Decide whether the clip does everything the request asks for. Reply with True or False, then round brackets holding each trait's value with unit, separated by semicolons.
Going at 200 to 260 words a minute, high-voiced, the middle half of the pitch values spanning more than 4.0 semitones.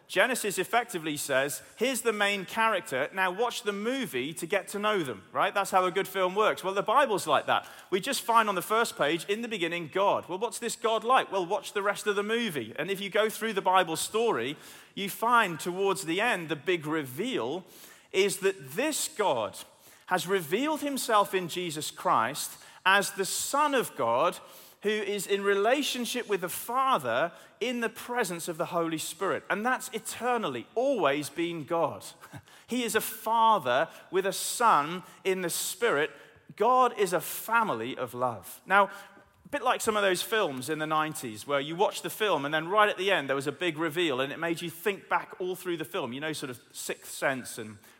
True (205 wpm; 195 Hz; 4.7 semitones)